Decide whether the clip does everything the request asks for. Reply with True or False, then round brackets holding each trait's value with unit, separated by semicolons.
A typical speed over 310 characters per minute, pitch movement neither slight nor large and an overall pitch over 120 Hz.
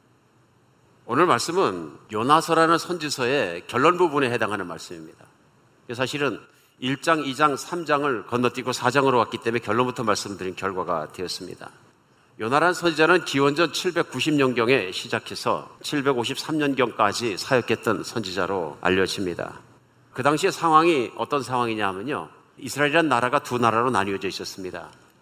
True (325 characters per minute; 4.8 semitones; 135 Hz)